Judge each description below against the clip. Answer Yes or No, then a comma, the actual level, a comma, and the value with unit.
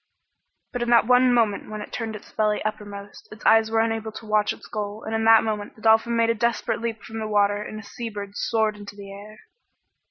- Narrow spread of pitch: Yes, narrow, 1.4 semitones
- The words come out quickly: Yes, fast, 230 wpm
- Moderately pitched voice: No, high, 215 Hz